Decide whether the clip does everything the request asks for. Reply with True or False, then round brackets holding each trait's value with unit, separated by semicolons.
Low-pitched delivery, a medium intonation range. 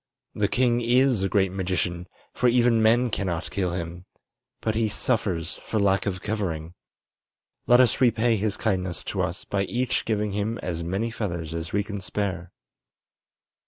True (100 Hz; 4.0 semitones)